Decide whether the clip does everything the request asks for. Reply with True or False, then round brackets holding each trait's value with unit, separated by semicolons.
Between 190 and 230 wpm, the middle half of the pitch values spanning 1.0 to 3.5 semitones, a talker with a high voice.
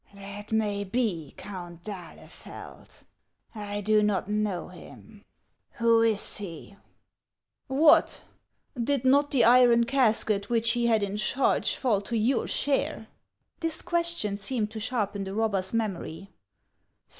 False (135 wpm; 3.0 semitones; 215 Hz)